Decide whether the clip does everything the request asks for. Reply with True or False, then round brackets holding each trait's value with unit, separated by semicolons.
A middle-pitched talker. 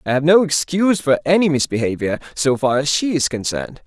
True (150 Hz)